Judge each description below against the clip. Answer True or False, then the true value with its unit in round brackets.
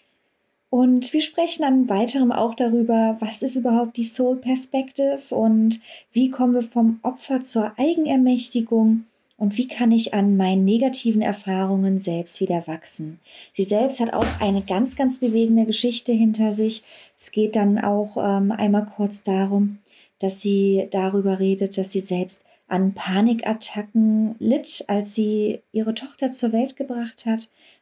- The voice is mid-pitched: False (225 Hz)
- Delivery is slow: False (145 wpm)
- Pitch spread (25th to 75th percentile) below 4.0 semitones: True (3.6 semitones)